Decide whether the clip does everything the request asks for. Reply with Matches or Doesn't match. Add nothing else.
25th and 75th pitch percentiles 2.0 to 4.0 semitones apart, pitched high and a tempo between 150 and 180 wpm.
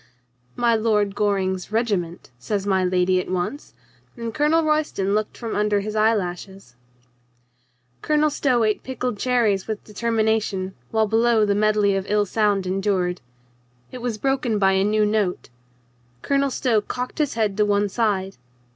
Matches